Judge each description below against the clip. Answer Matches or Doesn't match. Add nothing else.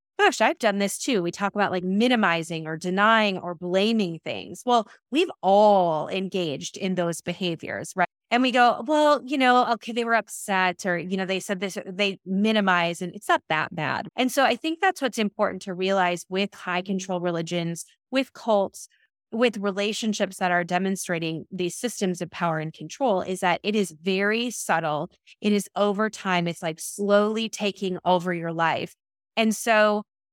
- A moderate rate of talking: Matches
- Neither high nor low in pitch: Doesn't match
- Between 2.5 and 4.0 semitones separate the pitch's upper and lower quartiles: Matches